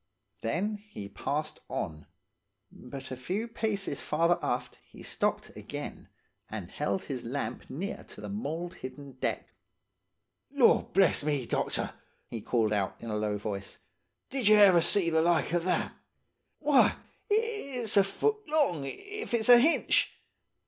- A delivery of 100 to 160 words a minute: Yes, average, 150 wpm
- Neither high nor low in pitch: Yes, medium, 175 Hz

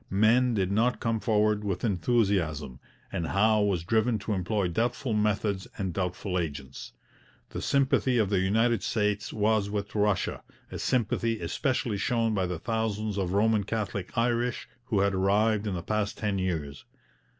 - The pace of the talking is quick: No, average, 160 wpm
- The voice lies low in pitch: Yes, low, 105 Hz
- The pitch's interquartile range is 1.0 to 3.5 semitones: Yes, average, 2.8 semitones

